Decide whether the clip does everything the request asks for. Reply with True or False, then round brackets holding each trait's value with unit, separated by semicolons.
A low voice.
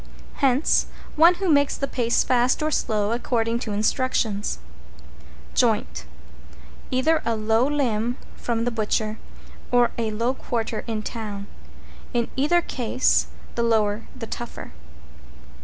False (235 Hz)